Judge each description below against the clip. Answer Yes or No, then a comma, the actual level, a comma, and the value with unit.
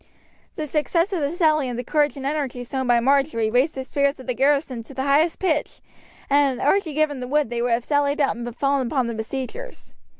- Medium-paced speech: No, fast, 230 wpm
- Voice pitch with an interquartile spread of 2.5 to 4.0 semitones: Yes, average, 3.2 semitones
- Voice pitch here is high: Yes, very high, 275 Hz